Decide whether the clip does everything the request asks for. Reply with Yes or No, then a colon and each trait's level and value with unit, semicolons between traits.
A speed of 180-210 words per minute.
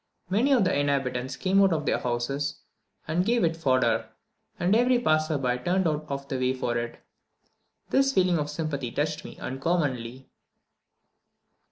No: average, 160 wpm